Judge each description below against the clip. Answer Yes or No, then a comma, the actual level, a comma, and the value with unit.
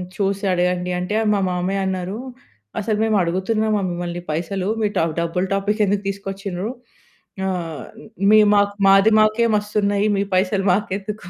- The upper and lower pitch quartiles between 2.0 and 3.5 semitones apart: Yes, narrow, 2.4 semitones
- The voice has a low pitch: No, high, 195 Hz